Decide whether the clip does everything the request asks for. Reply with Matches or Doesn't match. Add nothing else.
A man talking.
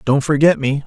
Matches